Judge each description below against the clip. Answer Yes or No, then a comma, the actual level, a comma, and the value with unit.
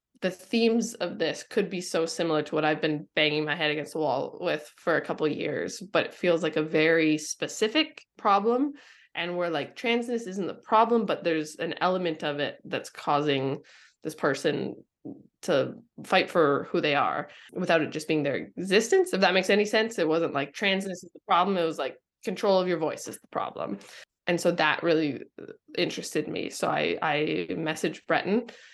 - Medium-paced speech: Yes, average, 195 wpm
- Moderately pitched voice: Yes, medium, 170 Hz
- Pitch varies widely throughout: No, average, 4.3 semitones